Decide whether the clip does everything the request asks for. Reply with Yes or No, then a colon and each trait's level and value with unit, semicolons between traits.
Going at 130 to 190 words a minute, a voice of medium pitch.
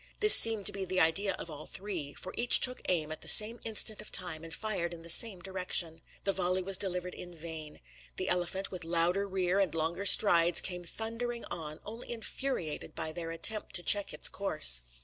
No: fast, 205 wpm; medium, 180 Hz